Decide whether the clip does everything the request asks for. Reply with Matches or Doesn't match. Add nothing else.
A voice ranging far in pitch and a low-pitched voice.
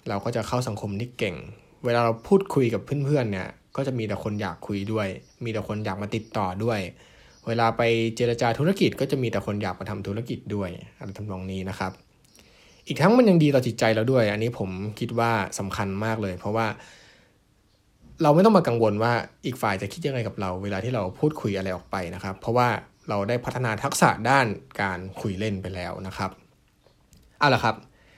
Doesn't match